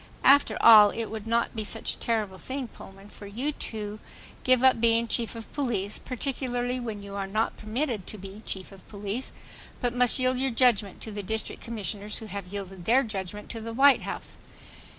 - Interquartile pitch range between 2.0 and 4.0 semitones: Yes, average, 3.3 semitones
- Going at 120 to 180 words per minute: No, average, 195 wpm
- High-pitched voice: Yes, high, 220 Hz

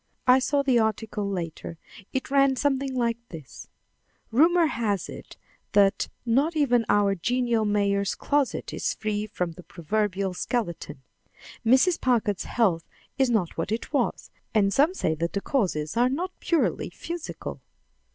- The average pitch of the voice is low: No, high, 225 Hz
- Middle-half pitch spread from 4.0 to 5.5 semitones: Yes, average, 5.1 semitones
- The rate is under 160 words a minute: Yes, average, 145 wpm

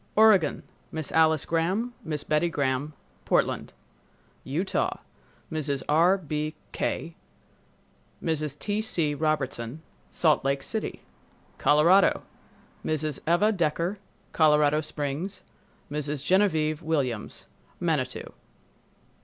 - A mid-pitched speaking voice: Yes, medium, 155 Hz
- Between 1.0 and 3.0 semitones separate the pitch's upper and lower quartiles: Yes, average, 2.7 semitones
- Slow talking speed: Yes, slow, 85 wpm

